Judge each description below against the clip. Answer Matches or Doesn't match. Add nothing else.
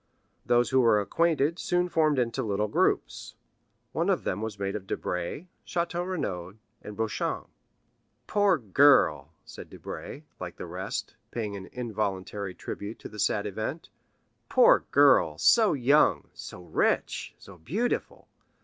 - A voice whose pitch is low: Matches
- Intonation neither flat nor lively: Doesn't match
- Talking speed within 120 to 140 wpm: Matches